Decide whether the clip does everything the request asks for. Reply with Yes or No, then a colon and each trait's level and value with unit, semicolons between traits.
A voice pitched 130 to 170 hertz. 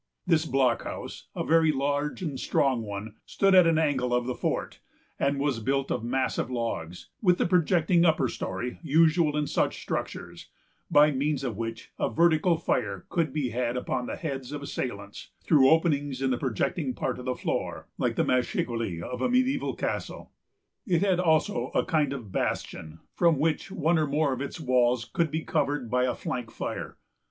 Yes: medium, 140 Hz